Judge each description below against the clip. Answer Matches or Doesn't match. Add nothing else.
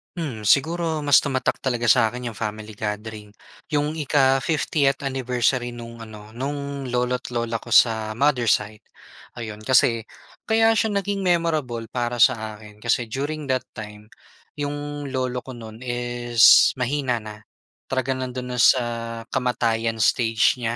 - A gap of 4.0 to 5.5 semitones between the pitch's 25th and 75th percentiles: Doesn't match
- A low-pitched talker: Matches